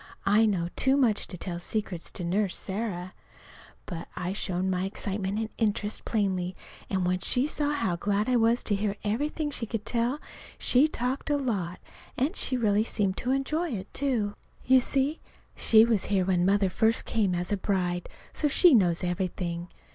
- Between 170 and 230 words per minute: Yes, average, 175 wpm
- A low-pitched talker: No, high, 205 Hz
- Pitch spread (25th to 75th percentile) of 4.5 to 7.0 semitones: Yes, average, 4.9 semitones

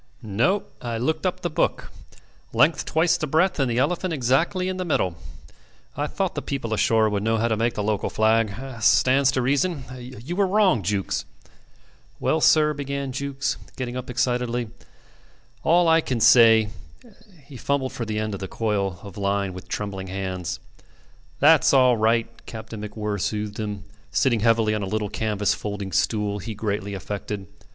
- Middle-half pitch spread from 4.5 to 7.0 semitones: Yes, average, 4.8 semitones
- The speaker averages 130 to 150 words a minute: No, average, 175 wpm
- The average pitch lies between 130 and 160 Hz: No, low, 115 Hz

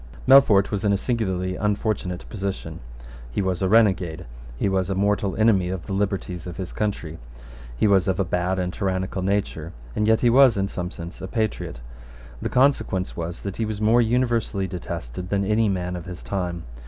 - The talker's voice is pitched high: No, very low, 95 Hz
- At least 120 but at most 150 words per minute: No, average, 190 wpm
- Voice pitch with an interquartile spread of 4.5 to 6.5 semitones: No, average, 2.8 semitones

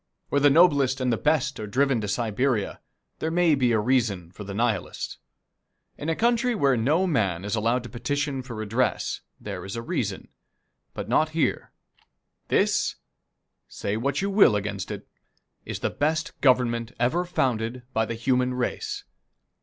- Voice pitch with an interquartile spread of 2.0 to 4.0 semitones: No, average, 4.9 semitones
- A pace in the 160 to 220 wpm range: Yes, average, 170 wpm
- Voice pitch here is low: Yes, low, 125 Hz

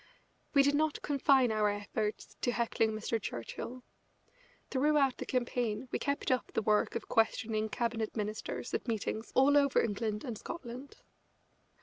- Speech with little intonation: No, average, 3.6 semitones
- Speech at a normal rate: Yes, average, 145 wpm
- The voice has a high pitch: Yes, high, 235 Hz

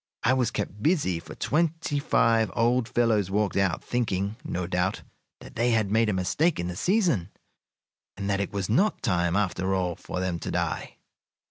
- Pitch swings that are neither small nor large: Yes, average, 4.7 semitones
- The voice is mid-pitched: No, low, 105 Hz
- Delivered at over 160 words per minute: Yes, average, 185 wpm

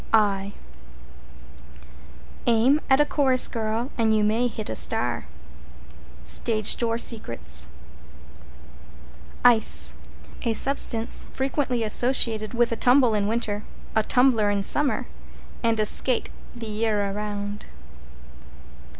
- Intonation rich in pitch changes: No, average, 2.8 semitones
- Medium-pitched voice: No, high, 225 Hz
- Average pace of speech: No, slow, 110 wpm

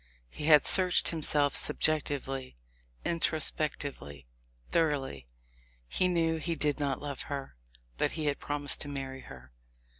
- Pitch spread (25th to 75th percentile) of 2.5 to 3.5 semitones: Yes, average, 2.8 semitones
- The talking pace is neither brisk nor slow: No, slow, 125 wpm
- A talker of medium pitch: Yes, medium, 145 Hz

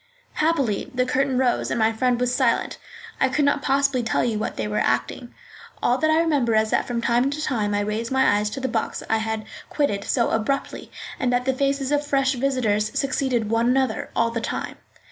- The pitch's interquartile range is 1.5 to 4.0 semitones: Yes, average, 3.6 semitones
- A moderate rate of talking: No, fast, 215 wpm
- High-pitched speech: Yes, very high, 250 Hz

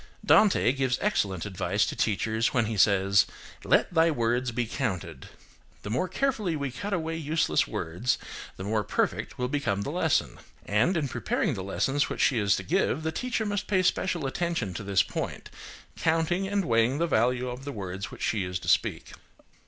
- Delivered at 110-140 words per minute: No, average, 185 wpm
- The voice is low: Yes, low, 125 Hz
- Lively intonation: Yes, wide, 8.3 semitones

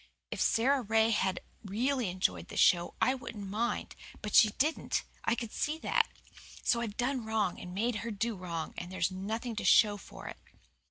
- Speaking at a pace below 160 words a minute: No, average, 185 wpm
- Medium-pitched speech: No, high, 220 Hz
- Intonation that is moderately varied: Yes, average, 3.9 semitones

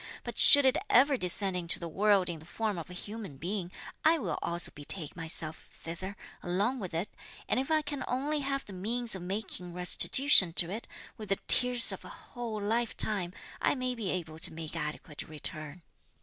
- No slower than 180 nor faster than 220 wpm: Yes, average, 190 wpm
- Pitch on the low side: No, high, 195 Hz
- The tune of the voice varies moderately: No, wide, 6.1 semitones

